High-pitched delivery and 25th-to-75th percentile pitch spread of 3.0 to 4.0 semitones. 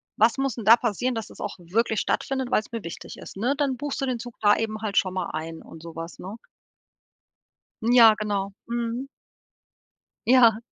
Yes: high, 225 Hz; average, 3.6 semitones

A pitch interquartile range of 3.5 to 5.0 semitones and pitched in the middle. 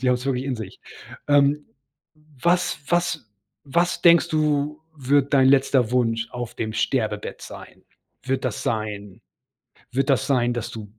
No: average, 3.8 semitones; low, 130 Hz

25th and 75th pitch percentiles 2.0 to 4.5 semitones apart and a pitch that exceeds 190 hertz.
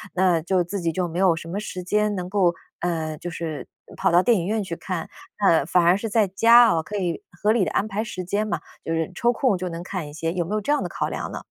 No: average, 3.5 semitones; medium, 185 Hz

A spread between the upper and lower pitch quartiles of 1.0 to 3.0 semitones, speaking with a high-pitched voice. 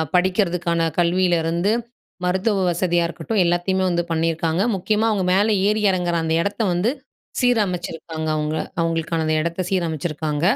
No: narrow, 2.4 semitones; medium, 175 Hz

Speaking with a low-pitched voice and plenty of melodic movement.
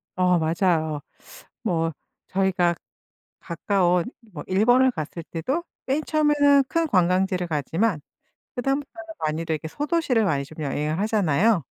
No: medium, 185 Hz; wide, 7.5 semitones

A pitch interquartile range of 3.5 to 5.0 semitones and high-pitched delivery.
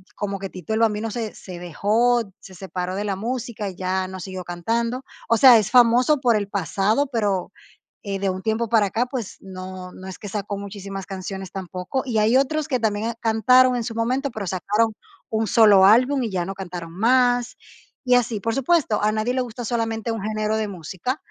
Yes: average, 3.8 semitones; high, 215 Hz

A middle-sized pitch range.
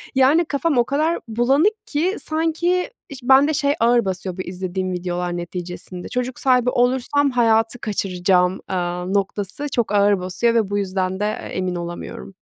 No: wide, 6.5 semitones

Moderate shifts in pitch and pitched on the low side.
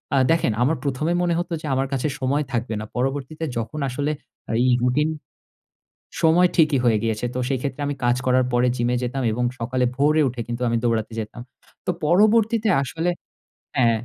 Yes: average, 4.2 semitones; low, 130 Hz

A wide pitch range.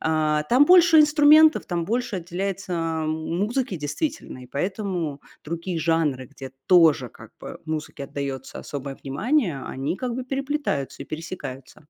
Yes: wide, 8.9 semitones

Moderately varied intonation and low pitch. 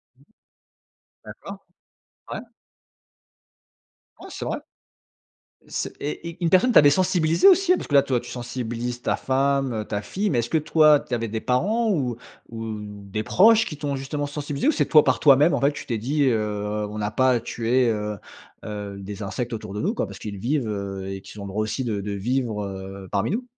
No: wide, 5.9 semitones; low, 125 Hz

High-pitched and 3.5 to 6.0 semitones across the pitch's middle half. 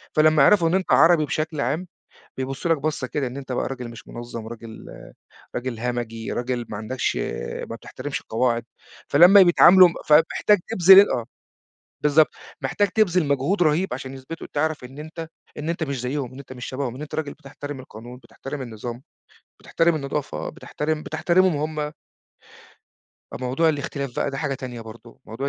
No: medium, 140 Hz; average, 4.1 semitones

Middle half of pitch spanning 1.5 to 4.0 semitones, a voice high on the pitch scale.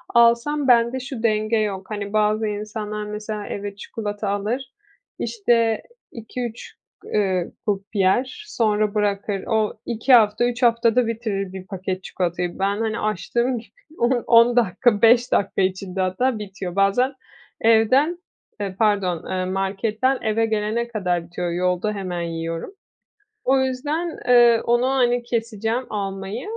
Yes: average, 3.4 semitones; high, 215 Hz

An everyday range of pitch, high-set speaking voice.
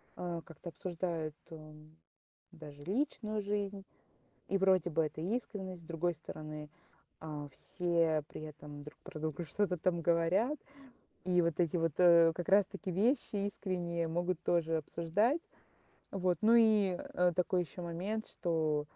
No: average, 3.2 semitones; medium, 175 Hz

